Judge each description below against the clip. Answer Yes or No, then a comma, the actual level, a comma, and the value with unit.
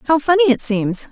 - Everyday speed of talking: No, fast, 215 wpm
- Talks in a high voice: Yes, very high, 275 Hz